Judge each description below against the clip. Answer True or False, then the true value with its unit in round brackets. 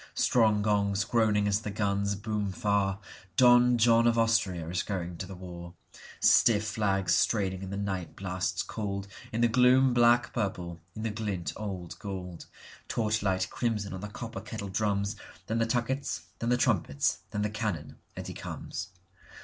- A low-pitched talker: True (105 Hz)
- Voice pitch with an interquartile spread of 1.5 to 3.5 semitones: True (3.0 semitones)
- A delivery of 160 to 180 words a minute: False (150 wpm)